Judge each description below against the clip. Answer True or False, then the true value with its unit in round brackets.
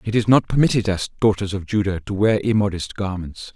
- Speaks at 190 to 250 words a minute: True (200 wpm)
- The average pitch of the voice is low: True (100 Hz)